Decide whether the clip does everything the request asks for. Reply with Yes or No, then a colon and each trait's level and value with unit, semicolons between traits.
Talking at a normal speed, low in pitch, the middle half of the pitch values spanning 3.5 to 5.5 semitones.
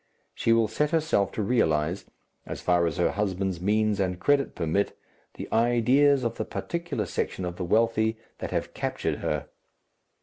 Yes: average, 165 wpm; low, 110 Hz; average, 5.0 semitones